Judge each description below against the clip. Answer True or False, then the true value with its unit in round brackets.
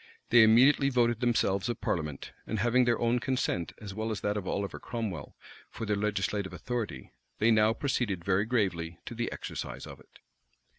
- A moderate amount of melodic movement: True (3.3 semitones)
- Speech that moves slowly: False (180 wpm)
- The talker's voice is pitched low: True (110 Hz)